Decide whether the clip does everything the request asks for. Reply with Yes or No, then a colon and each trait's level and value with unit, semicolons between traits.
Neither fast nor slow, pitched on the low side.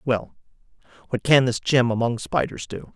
Yes: average, 165 wpm; low, 120 Hz